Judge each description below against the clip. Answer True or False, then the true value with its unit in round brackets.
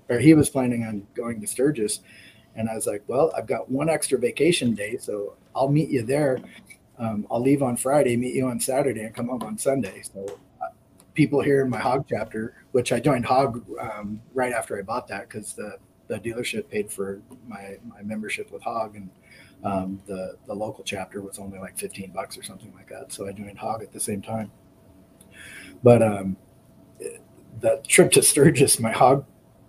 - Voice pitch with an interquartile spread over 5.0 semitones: True (5.4 semitones)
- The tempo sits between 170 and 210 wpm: True (200 wpm)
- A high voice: False (120 Hz)